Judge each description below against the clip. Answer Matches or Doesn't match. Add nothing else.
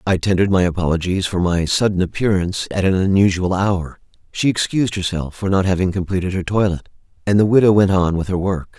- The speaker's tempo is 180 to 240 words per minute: Matches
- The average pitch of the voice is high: Doesn't match